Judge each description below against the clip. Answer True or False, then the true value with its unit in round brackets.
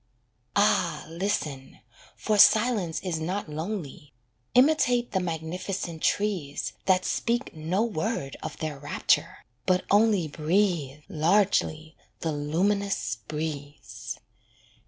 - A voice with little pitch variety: False (5.0 semitones)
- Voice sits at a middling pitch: True (170 Hz)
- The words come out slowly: True (100 wpm)